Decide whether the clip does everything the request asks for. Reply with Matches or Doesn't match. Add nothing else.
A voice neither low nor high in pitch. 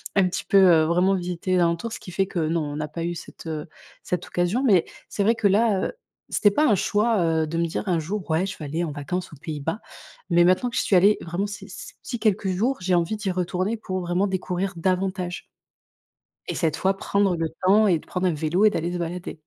Matches